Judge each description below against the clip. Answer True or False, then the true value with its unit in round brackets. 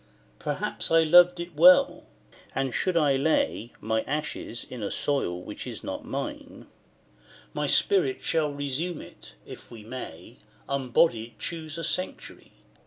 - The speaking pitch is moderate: True (145 Hz)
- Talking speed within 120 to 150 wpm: True (140 wpm)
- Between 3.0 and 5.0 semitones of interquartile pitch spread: False (5.5 semitones)